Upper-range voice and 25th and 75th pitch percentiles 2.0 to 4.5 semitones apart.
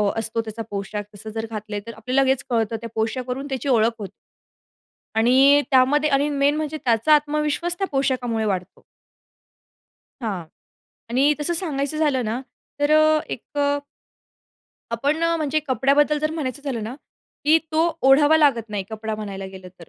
No: very high, 265 Hz; average, 4.9 semitones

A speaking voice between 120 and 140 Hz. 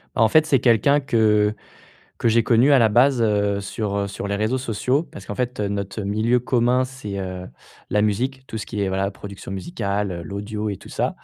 No: low, 105 Hz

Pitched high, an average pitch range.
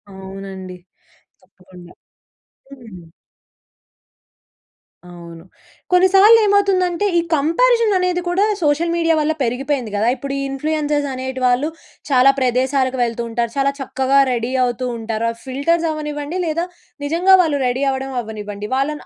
No: very high, 270 Hz; wide, 5.9 semitones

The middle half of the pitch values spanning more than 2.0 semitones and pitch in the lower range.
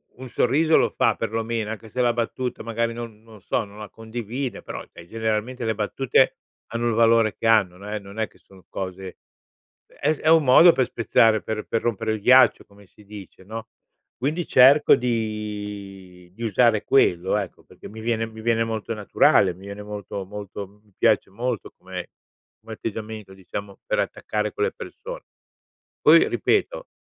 Yes: narrow, 2.5 semitones; low, 110 Hz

